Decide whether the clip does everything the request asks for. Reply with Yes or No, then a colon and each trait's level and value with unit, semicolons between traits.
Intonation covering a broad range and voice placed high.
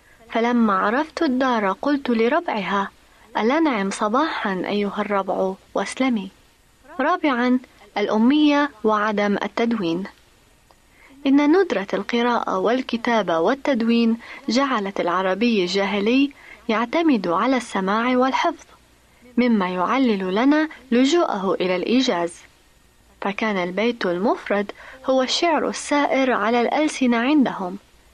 No: average, 4.9 semitones; high, 235 Hz